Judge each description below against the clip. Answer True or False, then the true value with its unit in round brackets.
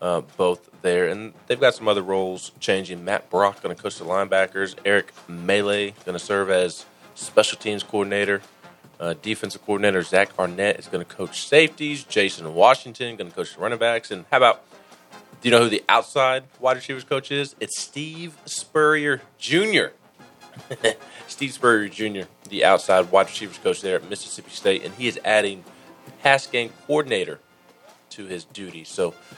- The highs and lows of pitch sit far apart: True (6.8 semitones)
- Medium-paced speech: True (170 wpm)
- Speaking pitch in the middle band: False (120 Hz)